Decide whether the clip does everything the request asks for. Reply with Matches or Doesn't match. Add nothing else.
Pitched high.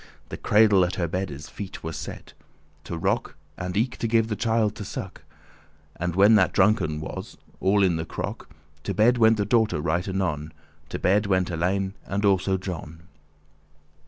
Doesn't match